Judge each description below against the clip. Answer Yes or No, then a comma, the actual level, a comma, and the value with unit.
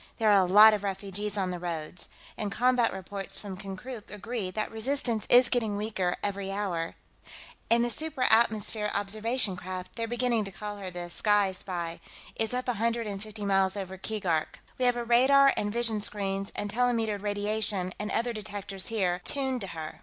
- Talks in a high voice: Yes, high, 210 Hz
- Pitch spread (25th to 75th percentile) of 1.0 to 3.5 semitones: Yes, average, 3.1 semitones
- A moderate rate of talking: Yes, average, 185 wpm